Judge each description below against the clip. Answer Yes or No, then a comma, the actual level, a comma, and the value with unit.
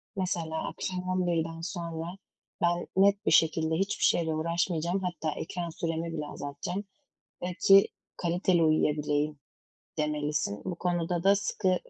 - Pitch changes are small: Yes, narrow, 2.3 semitones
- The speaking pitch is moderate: Yes, medium, 170 Hz